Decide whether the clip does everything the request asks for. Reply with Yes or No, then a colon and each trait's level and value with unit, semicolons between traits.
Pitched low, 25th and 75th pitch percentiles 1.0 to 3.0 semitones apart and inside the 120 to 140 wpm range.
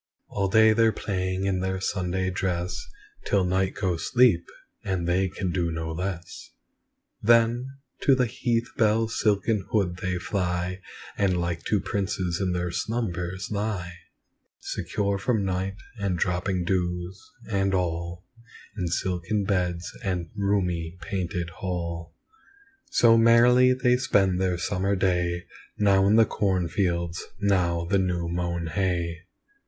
Yes: very low, 95 Hz; narrow, 2.5 semitones; slow, 135 wpm